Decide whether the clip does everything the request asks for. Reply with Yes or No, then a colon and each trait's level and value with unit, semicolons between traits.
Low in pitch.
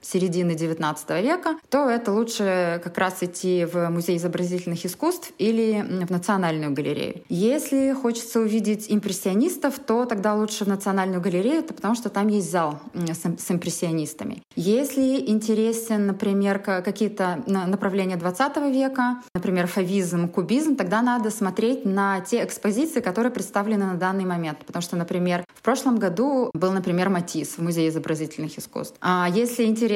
No: high, 195 Hz